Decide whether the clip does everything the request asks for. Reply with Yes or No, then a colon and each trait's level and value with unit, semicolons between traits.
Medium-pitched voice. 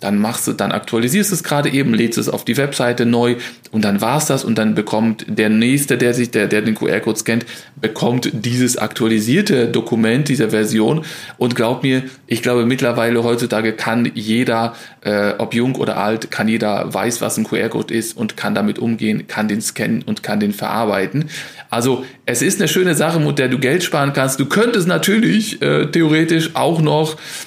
No: low, 120 Hz